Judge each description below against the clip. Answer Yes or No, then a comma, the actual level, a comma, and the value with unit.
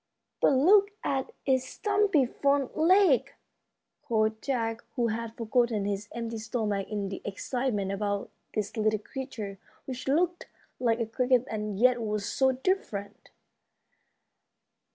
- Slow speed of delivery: Yes, slow, 130 wpm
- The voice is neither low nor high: No, high, 235 Hz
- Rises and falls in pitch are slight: No, average, 4.0 semitones